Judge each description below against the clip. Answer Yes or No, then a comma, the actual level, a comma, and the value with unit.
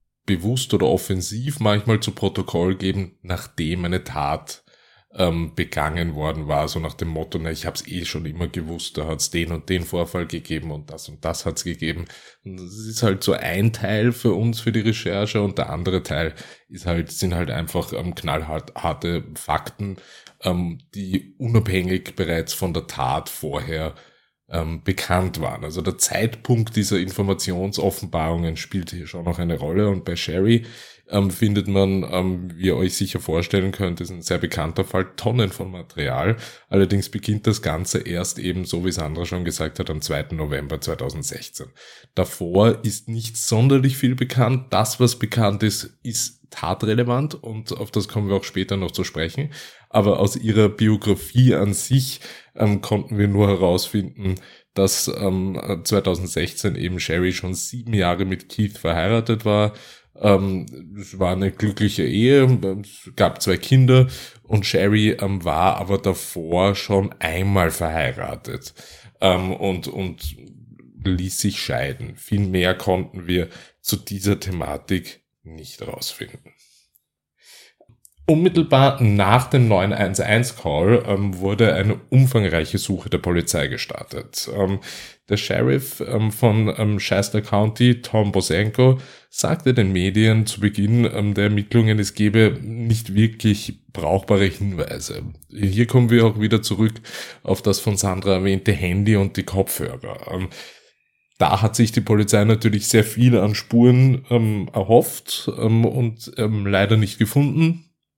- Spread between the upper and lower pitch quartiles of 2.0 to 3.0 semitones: No, average, 3.5 semitones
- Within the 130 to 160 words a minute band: Yes, average, 150 wpm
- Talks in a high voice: No, low, 100 Hz